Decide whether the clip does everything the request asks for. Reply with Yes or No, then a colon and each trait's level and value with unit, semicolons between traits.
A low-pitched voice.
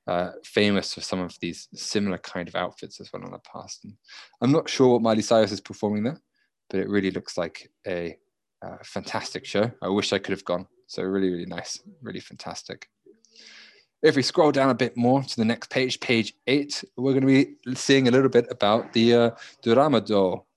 Yes: low, 115 Hz